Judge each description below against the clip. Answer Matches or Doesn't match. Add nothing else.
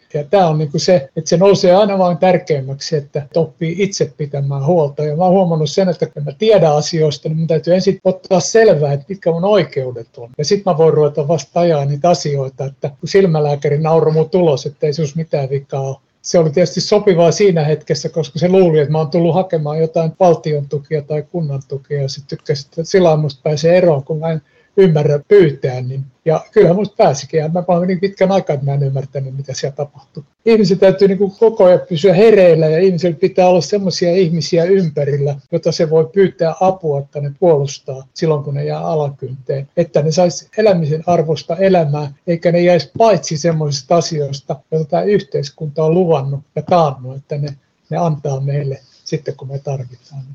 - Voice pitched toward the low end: Doesn't match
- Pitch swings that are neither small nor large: Matches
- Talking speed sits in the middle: Doesn't match